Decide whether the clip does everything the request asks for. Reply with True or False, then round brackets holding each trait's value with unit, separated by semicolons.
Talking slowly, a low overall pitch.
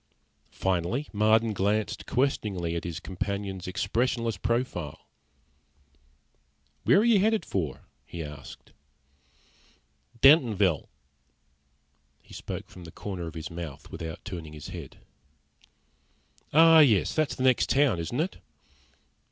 True (115 wpm; 100 Hz)